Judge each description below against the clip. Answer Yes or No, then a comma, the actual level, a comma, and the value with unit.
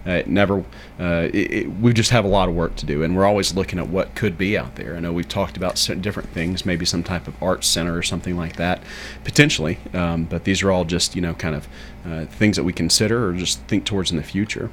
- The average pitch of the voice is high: No, very low, 90 Hz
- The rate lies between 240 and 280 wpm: Yes, fast, 265 wpm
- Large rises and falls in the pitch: No, narrow, 2.5 semitones